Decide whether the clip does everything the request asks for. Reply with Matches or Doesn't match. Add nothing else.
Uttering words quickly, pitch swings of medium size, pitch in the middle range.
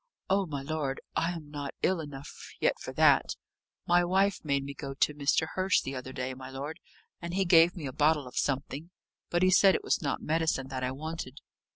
Matches